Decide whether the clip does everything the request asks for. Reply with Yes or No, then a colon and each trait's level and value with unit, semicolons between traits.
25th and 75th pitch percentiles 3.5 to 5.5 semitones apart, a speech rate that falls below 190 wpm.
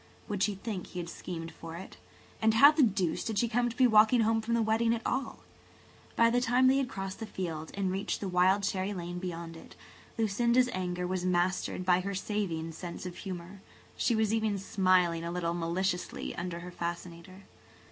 No: average, 3.9 semitones; average, 200 wpm